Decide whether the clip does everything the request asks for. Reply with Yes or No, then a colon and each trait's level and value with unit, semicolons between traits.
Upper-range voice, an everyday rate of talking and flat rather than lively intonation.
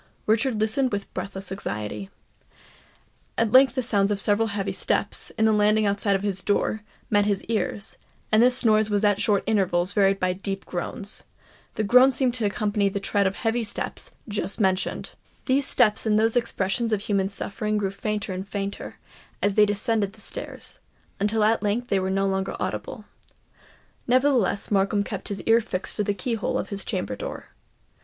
Yes: high, 205 Hz; average, 180 wpm; narrow, 2.2 semitones